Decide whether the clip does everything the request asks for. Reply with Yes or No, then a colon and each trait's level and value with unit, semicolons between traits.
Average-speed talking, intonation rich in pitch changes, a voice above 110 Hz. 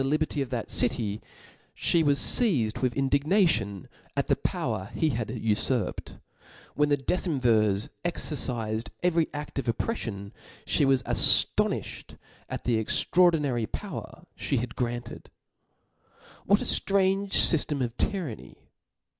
No: slow, 120 wpm; wide, 5.9 semitones; low, 135 Hz